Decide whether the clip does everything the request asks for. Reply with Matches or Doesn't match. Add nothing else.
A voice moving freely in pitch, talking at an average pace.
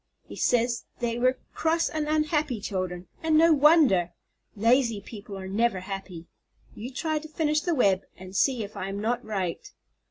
Matches